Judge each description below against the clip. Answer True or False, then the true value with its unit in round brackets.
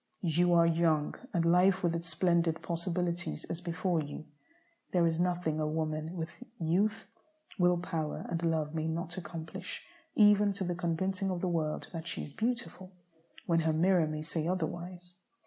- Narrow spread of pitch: True (1.9 semitones)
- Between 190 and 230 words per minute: False (165 wpm)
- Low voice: False (170 Hz)